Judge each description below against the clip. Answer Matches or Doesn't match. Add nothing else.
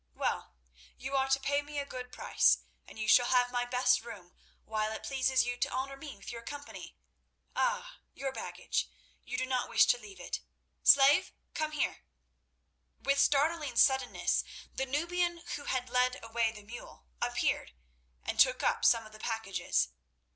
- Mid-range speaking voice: Doesn't match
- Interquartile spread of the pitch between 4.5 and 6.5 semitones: Doesn't match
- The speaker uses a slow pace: Doesn't match